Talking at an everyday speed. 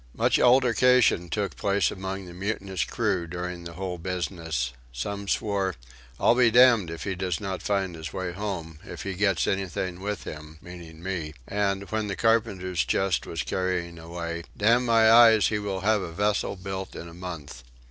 Yes: average, 180 wpm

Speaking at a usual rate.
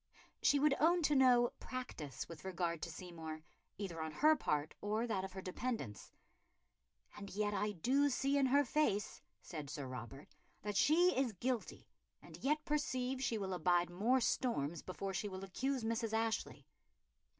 Yes: average, 165 wpm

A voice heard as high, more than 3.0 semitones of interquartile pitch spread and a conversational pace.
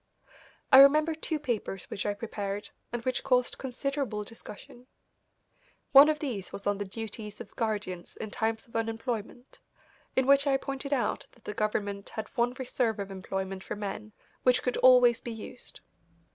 Yes: high, 230 Hz; average, 4.0 semitones; average, 165 wpm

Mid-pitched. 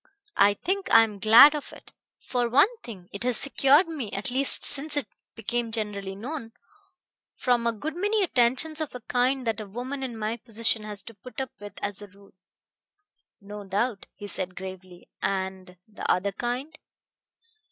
No: high, 230 Hz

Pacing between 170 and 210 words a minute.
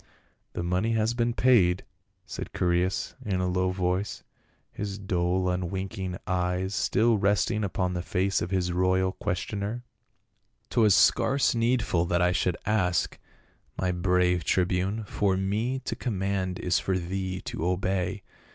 No: average, 150 wpm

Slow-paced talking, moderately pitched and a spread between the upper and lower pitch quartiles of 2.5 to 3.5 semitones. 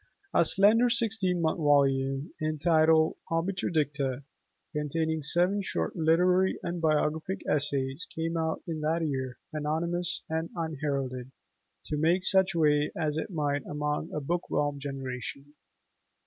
Yes: slow, 125 wpm; medium, 155 Hz; average, 2.8 semitones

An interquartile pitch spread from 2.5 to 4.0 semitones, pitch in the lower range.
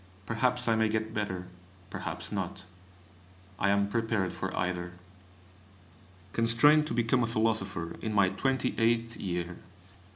Yes: average, 3.3 semitones; low, 110 Hz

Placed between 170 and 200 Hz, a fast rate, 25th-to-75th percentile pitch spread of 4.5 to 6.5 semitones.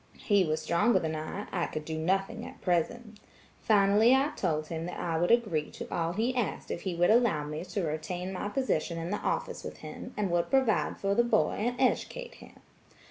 Yes: medium, 185 Hz; fast, 210 wpm; average, 5.2 semitones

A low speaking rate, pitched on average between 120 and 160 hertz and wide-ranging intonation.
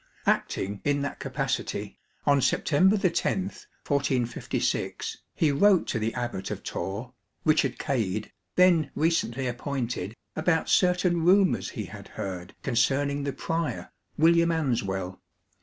Yes: slow, 120 wpm; medium, 140 Hz; wide, 5.9 semitones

